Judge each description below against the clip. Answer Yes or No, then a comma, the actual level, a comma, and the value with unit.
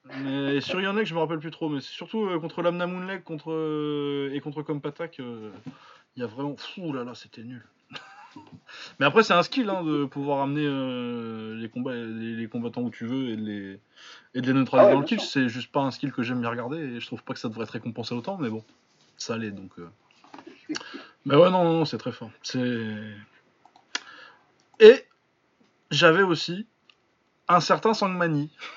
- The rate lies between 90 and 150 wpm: No, average, 205 wpm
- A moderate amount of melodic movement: No, wide, 6.0 semitones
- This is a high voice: No, medium, 140 Hz